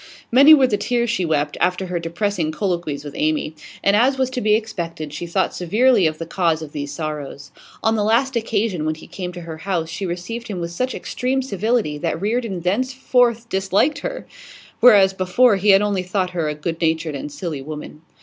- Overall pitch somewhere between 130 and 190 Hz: Yes, medium, 185 Hz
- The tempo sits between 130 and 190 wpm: No, fast, 205 wpm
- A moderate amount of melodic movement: No, wide, 6.0 semitones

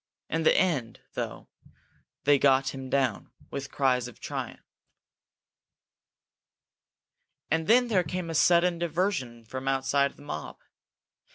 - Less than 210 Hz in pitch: Yes, medium, 140 Hz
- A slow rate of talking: Yes, slow, 120 wpm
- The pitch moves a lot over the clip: No, average, 4.5 semitones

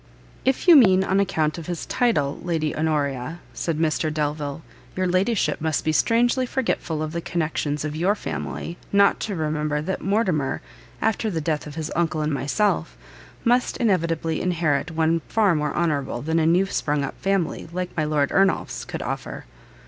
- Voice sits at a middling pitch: Yes, medium, 165 Hz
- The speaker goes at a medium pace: Yes, average, 170 wpm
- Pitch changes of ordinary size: Yes, average, 4.0 semitones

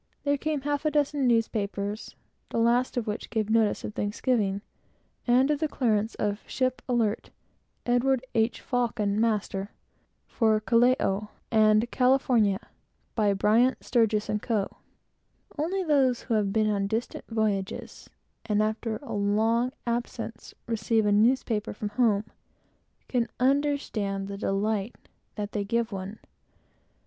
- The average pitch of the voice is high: Yes, high, 225 Hz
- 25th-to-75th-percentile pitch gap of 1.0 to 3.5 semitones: Yes, average, 3.0 semitones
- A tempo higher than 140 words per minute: No, slow, 135 wpm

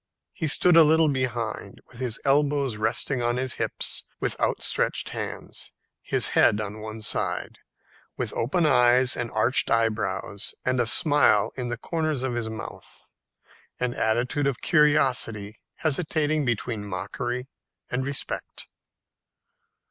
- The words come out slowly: Yes, slow, 130 wpm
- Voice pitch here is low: Yes, low, 125 Hz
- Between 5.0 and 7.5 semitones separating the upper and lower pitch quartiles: No, average, 4.2 semitones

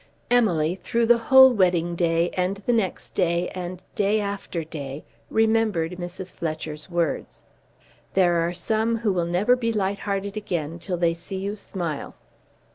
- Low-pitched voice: No, medium, 185 Hz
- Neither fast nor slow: Yes, average, 155 wpm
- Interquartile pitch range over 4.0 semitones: No, average, 3.7 semitones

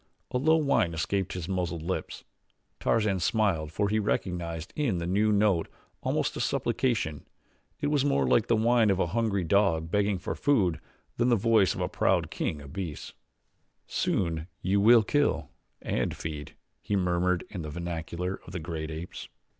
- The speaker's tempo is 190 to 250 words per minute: No, average, 170 wpm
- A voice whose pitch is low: Yes, very low, 95 Hz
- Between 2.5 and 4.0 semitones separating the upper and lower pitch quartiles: No, average, 4.5 semitones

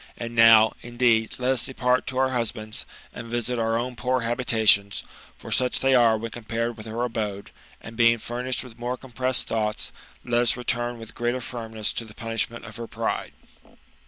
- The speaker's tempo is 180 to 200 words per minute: Yes, average, 185 wpm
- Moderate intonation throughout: No, narrow, 1.6 semitones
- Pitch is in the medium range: No, low, 120 Hz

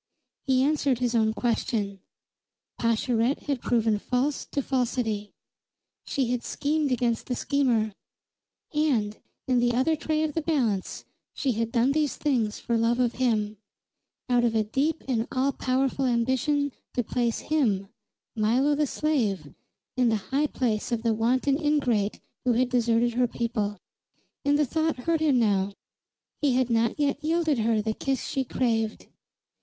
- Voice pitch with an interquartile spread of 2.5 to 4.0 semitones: Yes, average, 3.7 semitones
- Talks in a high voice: Yes, high, 245 Hz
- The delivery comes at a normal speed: Yes, average, 155 wpm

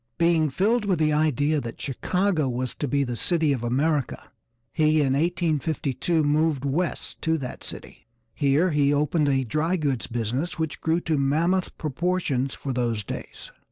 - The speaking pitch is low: No, medium, 150 Hz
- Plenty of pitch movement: No, average, 3.4 semitones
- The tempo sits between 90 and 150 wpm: No, average, 160 wpm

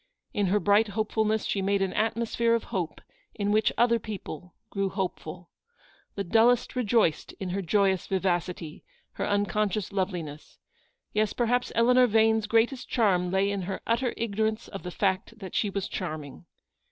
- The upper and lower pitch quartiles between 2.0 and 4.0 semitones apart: Yes, average, 3.0 semitones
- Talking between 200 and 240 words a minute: No, average, 160 wpm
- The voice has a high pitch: Yes, high, 205 Hz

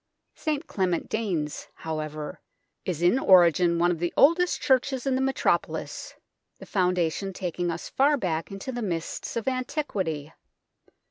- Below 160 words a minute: Yes, average, 140 wpm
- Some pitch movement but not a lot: No, wide, 7.6 semitones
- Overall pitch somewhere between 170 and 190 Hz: Yes, medium, 185 Hz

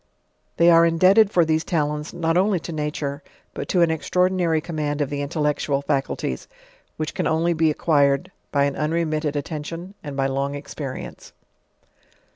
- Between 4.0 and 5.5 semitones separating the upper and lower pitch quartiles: No, average, 2.7 semitones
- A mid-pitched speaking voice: Yes, medium, 155 Hz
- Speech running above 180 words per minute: No, average, 155 wpm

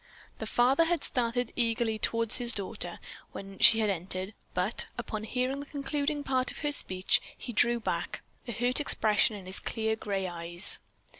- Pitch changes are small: No, average, 4.1 semitones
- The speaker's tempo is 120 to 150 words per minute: No, average, 170 wpm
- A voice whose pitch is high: Yes, high, 230 Hz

